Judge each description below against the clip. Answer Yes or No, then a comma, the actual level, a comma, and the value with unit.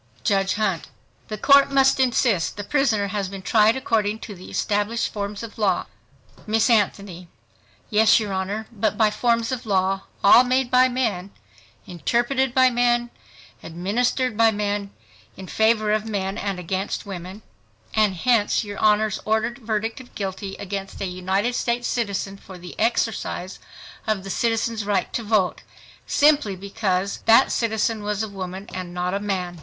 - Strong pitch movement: No, average, 3.1 semitones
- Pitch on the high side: Yes, high, 210 Hz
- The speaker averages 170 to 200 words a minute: No, average, 155 wpm